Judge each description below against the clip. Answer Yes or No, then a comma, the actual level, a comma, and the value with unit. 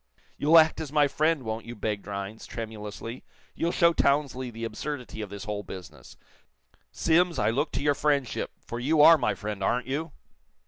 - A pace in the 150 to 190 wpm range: Yes, average, 180 wpm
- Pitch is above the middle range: No, low, 125 Hz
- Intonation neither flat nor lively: No, wide, 5.8 semitones